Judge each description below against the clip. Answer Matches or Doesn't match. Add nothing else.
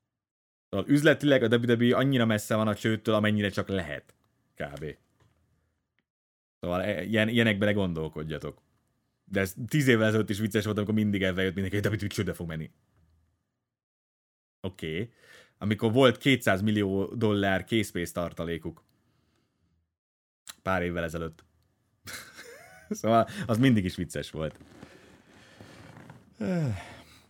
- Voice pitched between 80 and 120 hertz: Matches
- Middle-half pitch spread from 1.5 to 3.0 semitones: Doesn't match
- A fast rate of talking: Doesn't match